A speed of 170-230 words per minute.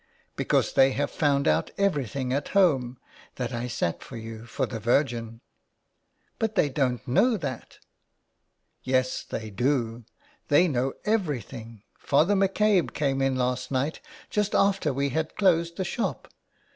No: average, 145 wpm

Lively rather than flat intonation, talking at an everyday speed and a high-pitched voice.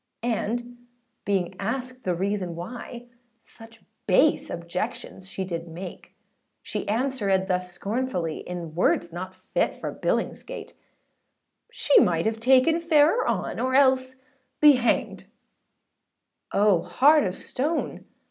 No: wide, 6.1 semitones; slow, 120 wpm; high, 220 Hz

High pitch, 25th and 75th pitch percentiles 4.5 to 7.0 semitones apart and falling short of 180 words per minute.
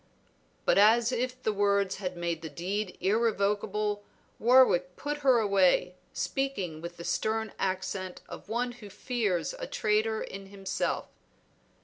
No: high, 205 Hz; average, 3.5 semitones; slow, 135 wpm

